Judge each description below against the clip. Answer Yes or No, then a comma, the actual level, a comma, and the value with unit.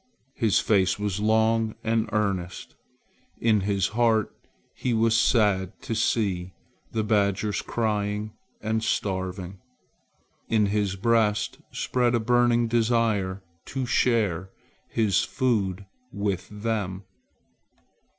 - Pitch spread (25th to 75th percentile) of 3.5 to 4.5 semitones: No, narrow, 2.5 semitones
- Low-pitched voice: Yes, low, 105 Hz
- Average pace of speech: No, slow, 105 wpm